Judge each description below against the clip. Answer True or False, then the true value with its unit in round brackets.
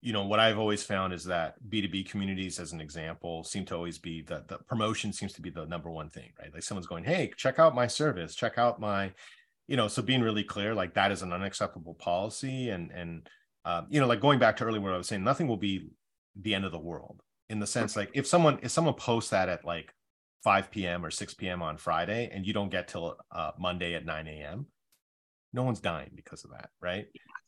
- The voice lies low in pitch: True (100 Hz)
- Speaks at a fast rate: True (240 wpm)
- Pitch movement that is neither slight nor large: True (5.0 semitones)